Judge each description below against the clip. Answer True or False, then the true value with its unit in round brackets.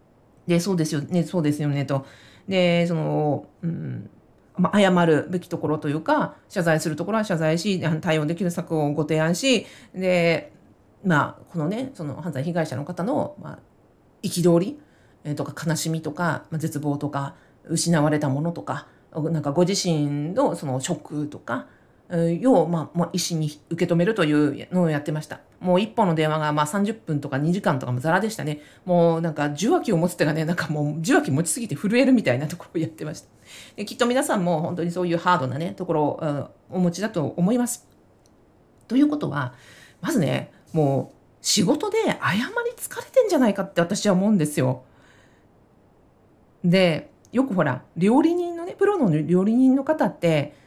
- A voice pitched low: False (165 Hz)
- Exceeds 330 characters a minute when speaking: False (300 characters per minute)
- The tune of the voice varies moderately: True (3.7 semitones)